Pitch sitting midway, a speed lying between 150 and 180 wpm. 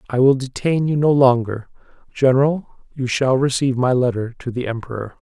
No: low, 130 Hz; average, 170 wpm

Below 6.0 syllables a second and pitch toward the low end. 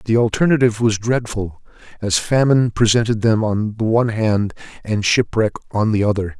Yes: 5.4 syllables/s; low, 110 Hz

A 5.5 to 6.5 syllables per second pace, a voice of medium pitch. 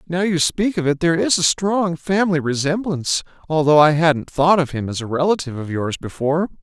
Yes: 5.7 syllables/s; medium, 160 Hz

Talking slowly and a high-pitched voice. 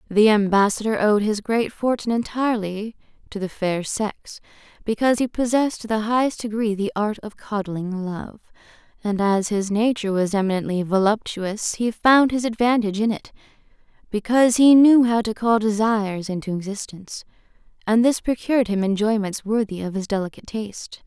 No: average, 155 wpm; high, 215 Hz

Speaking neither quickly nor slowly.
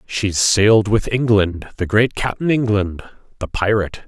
Yes: average, 145 wpm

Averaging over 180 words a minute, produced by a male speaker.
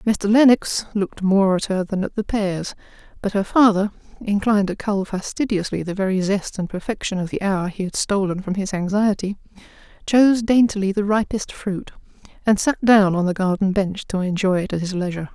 No: average, 190 wpm; female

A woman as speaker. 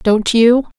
Yes: female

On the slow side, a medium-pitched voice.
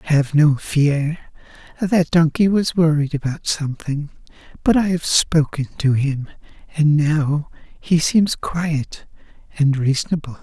Yes: slow, 125 wpm; medium, 155 Hz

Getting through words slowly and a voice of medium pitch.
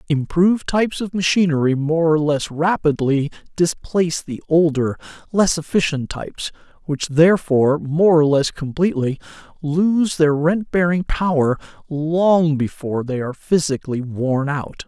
Yes: slow, 130 wpm; medium, 155 Hz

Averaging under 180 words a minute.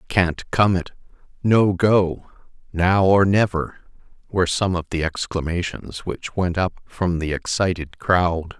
Yes: average, 140 wpm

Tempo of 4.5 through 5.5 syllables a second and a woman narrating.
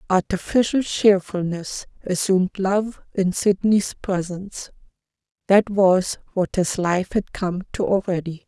No: 4.1 syllables/s; female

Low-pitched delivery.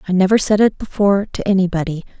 No: high, 190 Hz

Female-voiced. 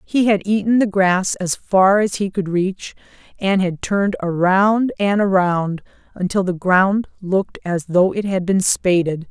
Yes: female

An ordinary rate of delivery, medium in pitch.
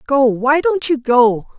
No: average, 150 wpm; very high, 255 Hz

